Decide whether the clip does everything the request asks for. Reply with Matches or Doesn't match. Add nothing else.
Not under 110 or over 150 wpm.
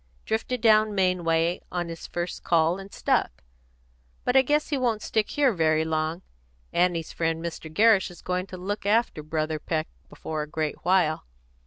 Doesn't match